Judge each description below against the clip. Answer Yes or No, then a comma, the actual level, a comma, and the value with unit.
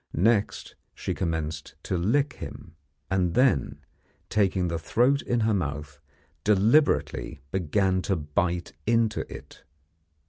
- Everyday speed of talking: No, slow, 115 wpm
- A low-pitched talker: Yes, very low, 95 Hz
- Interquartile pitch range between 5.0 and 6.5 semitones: Yes, average, 5.3 semitones